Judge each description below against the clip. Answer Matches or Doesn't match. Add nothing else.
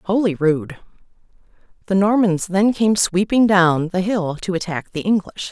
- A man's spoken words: Doesn't match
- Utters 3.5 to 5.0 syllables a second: Matches